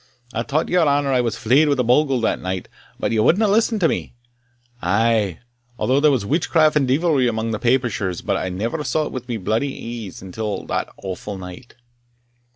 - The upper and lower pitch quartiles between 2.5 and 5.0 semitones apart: No, wide, 5.4 semitones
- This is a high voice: No, low, 120 Hz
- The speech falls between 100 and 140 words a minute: No, average, 190 wpm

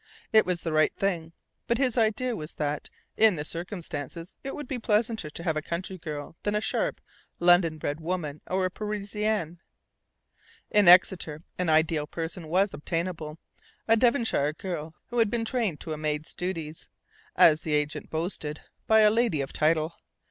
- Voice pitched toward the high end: No, medium, 175 Hz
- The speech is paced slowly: No, average, 170 wpm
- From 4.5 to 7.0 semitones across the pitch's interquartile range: Yes, average, 5.2 semitones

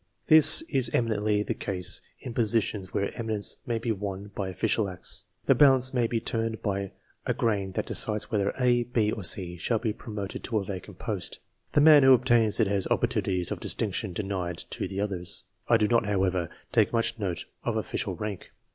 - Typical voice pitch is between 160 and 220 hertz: No, low, 105 Hz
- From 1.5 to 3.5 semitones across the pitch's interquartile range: Yes, average, 3.2 semitones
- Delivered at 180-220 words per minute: Yes, average, 190 wpm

